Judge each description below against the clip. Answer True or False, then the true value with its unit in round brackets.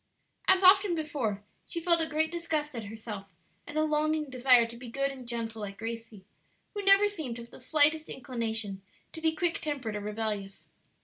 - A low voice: False (260 Hz)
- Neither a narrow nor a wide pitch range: False (6.0 semitones)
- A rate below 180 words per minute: False (190 wpm)